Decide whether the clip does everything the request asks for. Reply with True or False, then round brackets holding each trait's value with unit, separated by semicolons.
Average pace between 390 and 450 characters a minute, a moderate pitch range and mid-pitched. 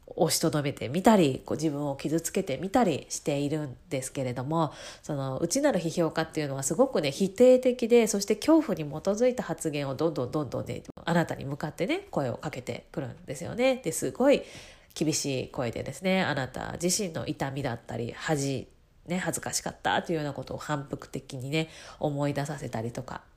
True (395 characters per minute; 4.7 semitones; 160 Hz)